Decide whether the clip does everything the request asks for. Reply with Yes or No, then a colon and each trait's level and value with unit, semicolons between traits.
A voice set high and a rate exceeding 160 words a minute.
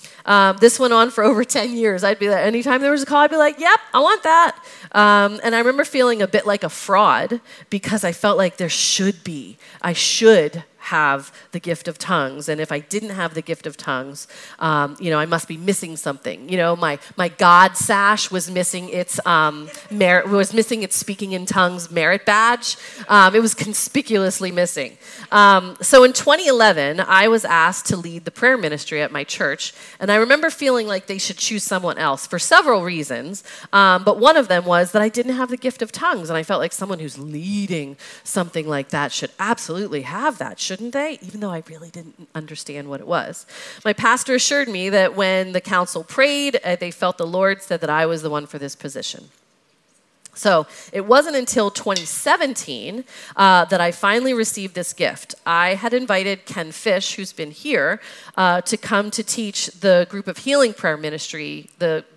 Yes: high, 195 Hz; fast, 205 wpm